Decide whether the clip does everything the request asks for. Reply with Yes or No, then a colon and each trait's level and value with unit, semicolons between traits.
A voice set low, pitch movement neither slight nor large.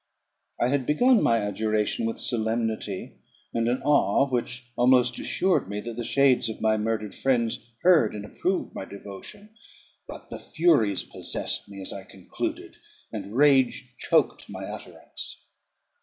Yes: low, 115 Hz; average, 4.2 semitones